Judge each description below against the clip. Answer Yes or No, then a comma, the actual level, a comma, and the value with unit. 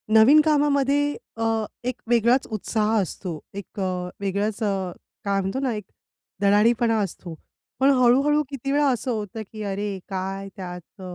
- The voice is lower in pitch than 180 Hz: No, high, 215 Hz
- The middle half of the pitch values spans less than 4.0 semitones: No, average, 4.5 semitones